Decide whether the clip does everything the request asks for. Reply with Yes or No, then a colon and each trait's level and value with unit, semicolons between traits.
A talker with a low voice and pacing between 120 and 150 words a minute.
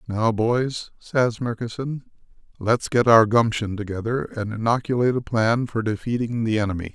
Yes: low, 115 Hz; average, 145 wpm